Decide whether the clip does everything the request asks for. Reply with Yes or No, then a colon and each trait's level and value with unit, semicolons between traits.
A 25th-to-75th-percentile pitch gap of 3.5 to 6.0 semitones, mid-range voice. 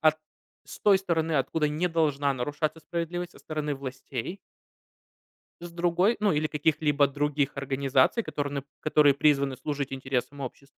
No: average, 2.8 semitones; medium, 150 Hz